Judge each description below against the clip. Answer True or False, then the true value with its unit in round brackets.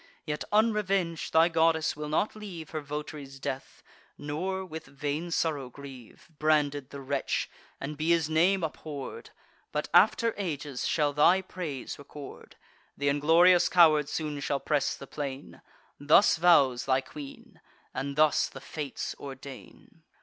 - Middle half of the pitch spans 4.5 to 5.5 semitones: False (2.9 semitones)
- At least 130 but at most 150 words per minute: True (140 wpm)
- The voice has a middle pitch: True (150 Hz)